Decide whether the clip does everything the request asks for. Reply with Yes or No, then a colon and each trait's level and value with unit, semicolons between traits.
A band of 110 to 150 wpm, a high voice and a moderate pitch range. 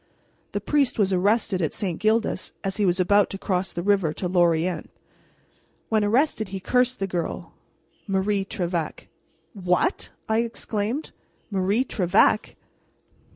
Yes: average, 140 wpm; high, 195 Hz; average, 3.2 semitones